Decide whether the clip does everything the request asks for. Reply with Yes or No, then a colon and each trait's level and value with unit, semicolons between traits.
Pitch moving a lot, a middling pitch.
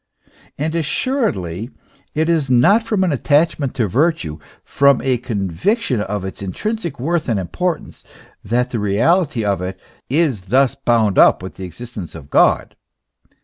No: wide, 8.2 semitones; low, 125 Hz